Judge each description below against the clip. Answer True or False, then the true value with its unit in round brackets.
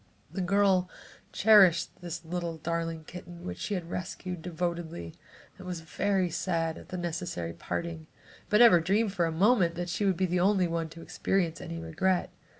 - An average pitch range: False (2.2 semitones)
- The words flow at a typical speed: True (180 wpm)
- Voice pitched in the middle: True (175 Hz)